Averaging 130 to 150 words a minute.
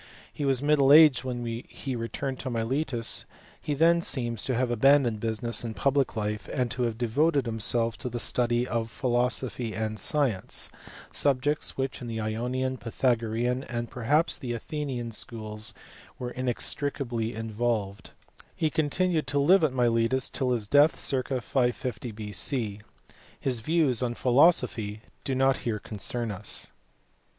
Yes: average, 145 wpm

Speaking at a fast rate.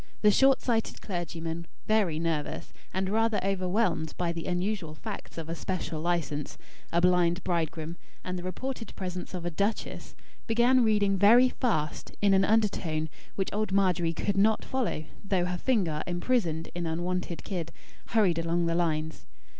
No: average, 155 wpm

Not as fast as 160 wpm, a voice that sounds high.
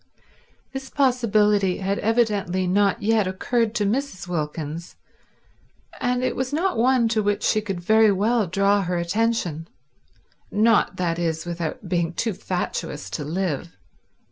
Yes: average, 140 wpm; high, 200 Hz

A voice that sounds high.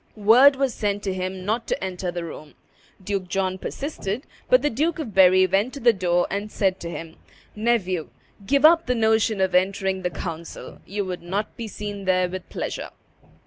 Yes: high, 195 Hz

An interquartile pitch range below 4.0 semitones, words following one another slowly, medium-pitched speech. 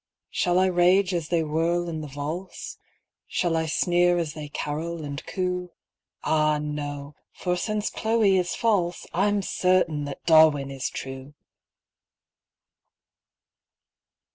Yes: average, 3.4 semitones; slow, 125 wpm; medium, 170 Hz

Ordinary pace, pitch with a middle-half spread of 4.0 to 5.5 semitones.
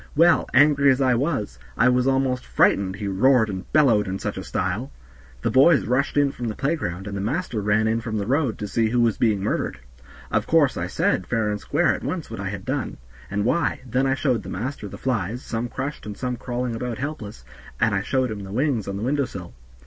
No: fast, 235 wpm; average, 4.3 semitones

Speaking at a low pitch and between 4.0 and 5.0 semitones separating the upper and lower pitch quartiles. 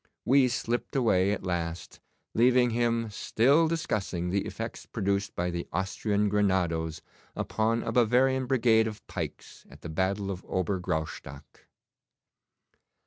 Yes: low, 105 Hz; average, 4.6 semitones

